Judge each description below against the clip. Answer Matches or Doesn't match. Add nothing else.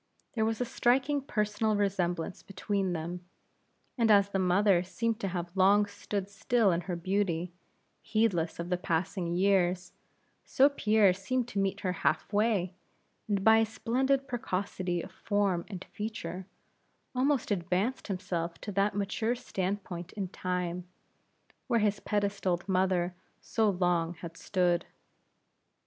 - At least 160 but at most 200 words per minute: Doesn't match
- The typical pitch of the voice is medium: Doesn't match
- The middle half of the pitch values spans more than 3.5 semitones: Doesn't match